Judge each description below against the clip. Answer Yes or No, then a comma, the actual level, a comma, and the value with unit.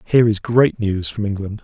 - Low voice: Yes, low, 105 Hz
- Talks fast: Yes, fast, 220 wpm